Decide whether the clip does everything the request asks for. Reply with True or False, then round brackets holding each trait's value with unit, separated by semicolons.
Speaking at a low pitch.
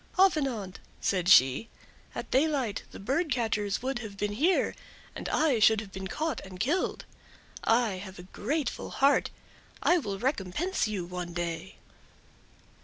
False (220 Hz)